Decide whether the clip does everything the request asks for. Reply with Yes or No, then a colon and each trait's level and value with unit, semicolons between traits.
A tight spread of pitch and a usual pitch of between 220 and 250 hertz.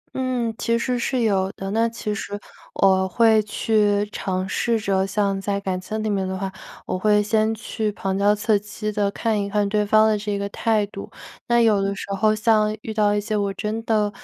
No: narrow, 1.6 semitones; high, 210 Hz